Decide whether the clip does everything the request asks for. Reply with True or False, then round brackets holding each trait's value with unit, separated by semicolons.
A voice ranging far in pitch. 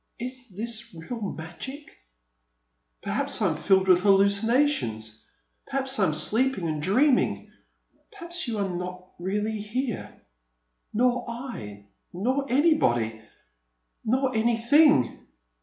True (6.5 semitones)